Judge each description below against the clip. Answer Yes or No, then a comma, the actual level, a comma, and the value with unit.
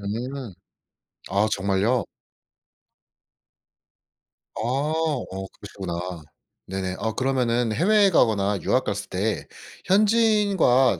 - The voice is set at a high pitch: No, low, 115 Hz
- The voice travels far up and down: Yes, wide, 6.9 semitones